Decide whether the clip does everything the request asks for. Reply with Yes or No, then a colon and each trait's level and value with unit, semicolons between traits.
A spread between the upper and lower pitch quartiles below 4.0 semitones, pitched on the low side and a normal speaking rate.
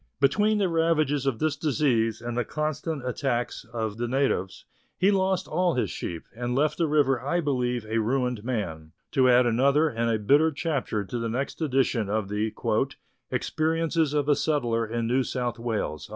No: average, 4.8 semitones; low, 130 Hz; average, 180 wpm